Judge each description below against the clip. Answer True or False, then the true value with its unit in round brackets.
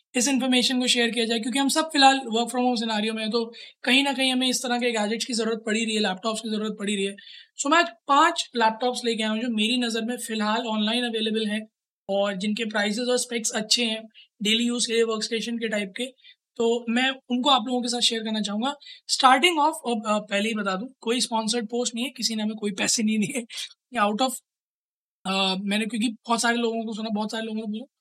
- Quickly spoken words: True (235 wpm)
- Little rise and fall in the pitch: True (2.3 semitones)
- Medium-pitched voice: False (230 Hz)